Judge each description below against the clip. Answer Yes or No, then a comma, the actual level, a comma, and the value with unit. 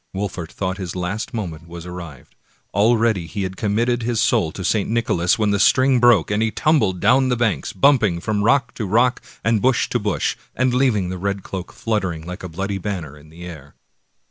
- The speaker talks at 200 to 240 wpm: Yes, fast, 205 wpm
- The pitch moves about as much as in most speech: Yes, average, 4.8 semitones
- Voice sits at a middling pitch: No, low, 100 Hz